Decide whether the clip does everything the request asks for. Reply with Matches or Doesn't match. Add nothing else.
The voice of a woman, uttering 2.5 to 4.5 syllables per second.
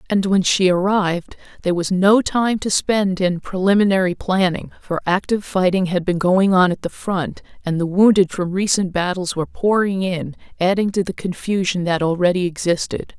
Doesn't match